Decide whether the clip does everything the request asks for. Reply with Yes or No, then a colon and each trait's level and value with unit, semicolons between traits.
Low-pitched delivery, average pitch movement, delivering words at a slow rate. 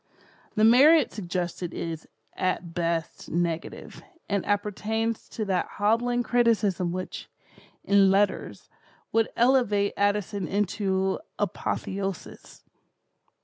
No: high, 200 Hz; average, 3.4 semitones; slow, 95 wpm